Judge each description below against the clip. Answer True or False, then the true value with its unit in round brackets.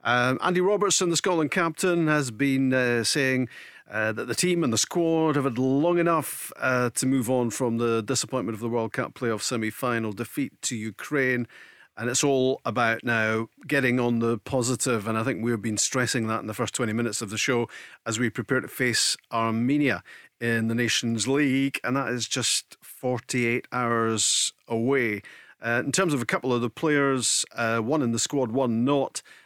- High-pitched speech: False (125 Hz)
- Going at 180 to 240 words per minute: True (195 wpm)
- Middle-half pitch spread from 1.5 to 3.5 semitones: True (3.0 semitones)